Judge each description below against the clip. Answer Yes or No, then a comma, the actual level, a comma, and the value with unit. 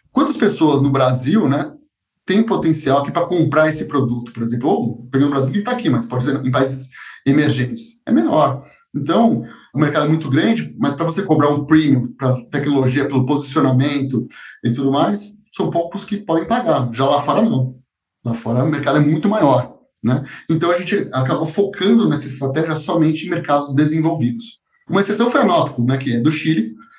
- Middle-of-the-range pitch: Yes, medium, 145 Hz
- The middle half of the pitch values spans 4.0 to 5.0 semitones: Yes, average, 4.5 semitones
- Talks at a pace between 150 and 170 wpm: No, average, 180 wpm